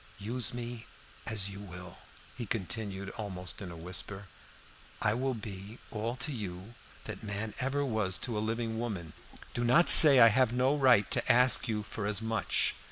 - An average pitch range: Yes, average, 3.6 semitones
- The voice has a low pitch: Yes, low, 110 Hz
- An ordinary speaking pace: Yes, average, 175 wpm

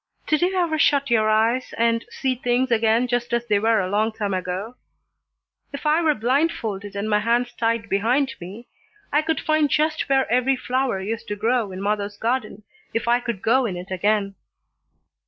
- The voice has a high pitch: Yes, high, 230 Hz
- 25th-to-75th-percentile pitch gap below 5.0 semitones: Yes, average, 3.9 semitones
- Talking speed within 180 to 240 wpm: Yes, average, 190 wpm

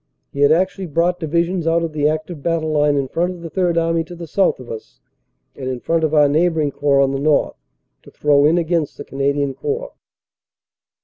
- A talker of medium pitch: Yes, medium, 155 Hz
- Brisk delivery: Yes, fast, 210 wpm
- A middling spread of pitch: Yes, average, 3.0 semitones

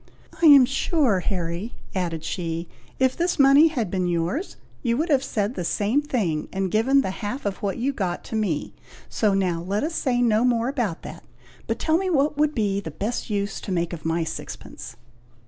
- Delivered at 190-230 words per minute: Yes, average, 200 wpm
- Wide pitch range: Yes, wide, 7.0 semitones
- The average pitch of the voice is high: Yes, high, 215 Hz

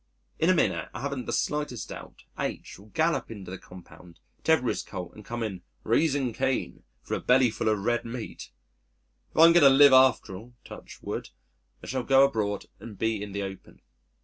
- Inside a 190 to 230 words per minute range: Yes, average, 200 wpm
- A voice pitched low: Yes, low, 120 Hz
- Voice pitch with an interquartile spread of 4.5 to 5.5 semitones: Yes, average, 5.1 semitones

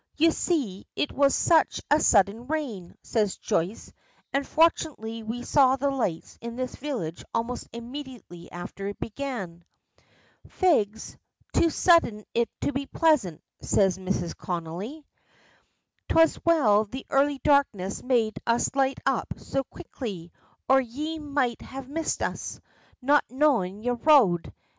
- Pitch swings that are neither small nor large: No, wide, 5.8 semitones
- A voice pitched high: Yes, very high, 250 Hz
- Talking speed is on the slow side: Yes, slow, 130 wpm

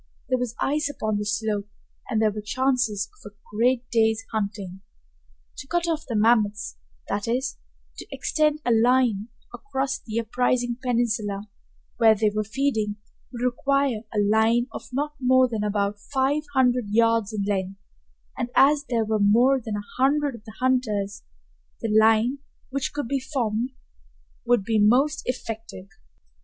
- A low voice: No, high, 230 Hz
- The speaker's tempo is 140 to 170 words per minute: Yes, average, 155 wpm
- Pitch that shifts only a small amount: No, average, 3.5 semitones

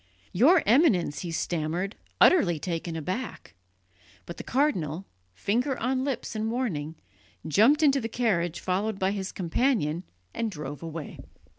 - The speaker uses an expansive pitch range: Yes, wide, 7.1 semitones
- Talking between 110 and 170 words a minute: Yes, slow, 135 wpm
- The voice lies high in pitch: Yes, high, 195 Hz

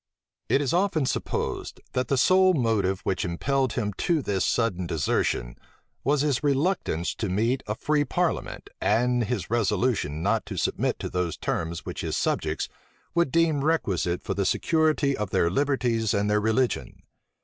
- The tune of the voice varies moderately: No, wide, 6.7 semitones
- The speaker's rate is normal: Yes, average, 160 wpm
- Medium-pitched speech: No, low, 120 Hz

